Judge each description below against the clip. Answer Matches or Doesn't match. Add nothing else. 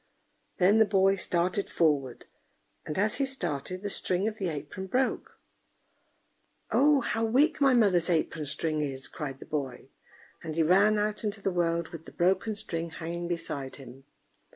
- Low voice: Doesn't match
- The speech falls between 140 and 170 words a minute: Matches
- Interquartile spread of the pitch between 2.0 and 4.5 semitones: Doesn't match